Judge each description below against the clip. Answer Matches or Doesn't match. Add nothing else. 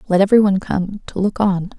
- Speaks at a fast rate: Matches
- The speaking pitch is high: Matches